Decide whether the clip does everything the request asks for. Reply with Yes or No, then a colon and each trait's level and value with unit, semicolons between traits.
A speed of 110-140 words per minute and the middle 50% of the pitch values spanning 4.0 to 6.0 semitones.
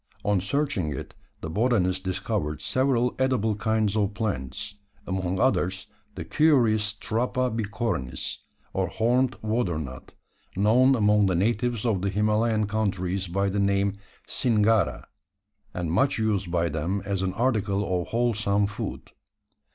No: slow, 135 wpm; average, 3.5 semitones